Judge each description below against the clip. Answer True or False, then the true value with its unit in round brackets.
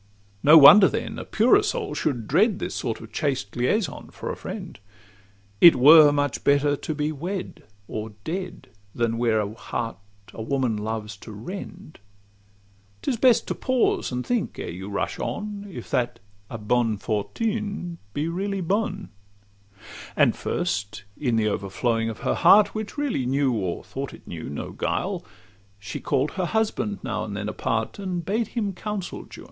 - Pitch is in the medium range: True (145 Hz)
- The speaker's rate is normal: True (165 wpm)